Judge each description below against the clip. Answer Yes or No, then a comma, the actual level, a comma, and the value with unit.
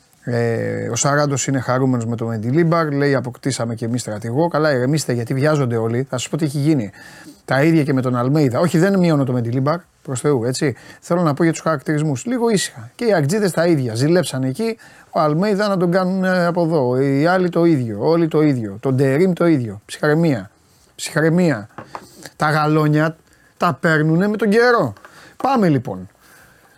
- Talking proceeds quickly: Yes, fast, 180 wpm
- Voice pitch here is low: No, medium, 150 Hz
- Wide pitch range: No, average, 4.9 semitones